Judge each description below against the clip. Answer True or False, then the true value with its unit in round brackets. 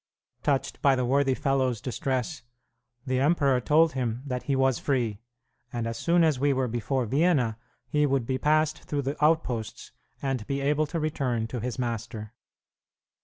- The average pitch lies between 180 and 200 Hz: False (135 Hz)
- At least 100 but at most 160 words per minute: False (170 wpm)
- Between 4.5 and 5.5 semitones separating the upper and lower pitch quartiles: False (3.2 semitones)